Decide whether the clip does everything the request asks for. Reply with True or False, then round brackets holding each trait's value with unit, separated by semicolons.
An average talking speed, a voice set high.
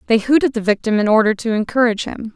False (255 wpm; 225 Hz)